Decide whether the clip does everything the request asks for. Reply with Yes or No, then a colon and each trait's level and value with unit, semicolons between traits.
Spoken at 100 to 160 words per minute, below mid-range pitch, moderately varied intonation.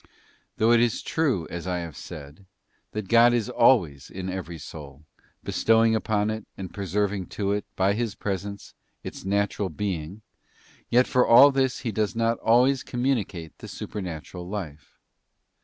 Yes: average, 155 wpm; low, 100 Hz; average, 4.3 semitones